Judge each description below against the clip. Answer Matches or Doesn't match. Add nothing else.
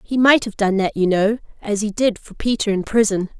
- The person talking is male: Doesn't match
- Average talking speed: Doesn't match